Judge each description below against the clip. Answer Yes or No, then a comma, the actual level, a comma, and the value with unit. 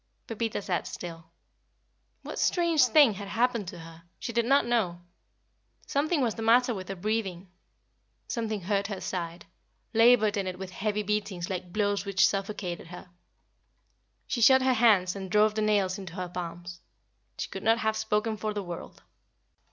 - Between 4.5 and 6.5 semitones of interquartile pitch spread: No, average, 3.7 semitones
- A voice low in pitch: No, high, 205 Hz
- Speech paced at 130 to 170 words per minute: Yes, average, 165 wpm